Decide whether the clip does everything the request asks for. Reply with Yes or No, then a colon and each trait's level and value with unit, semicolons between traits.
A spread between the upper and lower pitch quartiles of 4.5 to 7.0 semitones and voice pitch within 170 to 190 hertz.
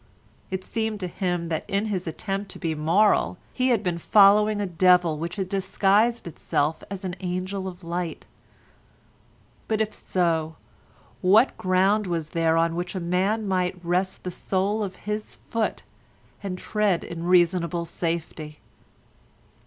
No: average, 2.9 semitones; medium, 185 Hz